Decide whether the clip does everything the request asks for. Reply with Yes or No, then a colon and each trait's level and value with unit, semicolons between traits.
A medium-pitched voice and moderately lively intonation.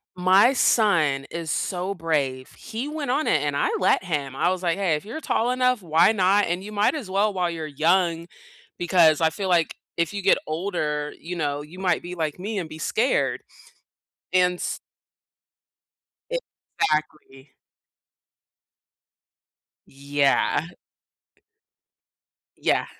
Yes: medium, 175 Hz; average, 4.5 semitones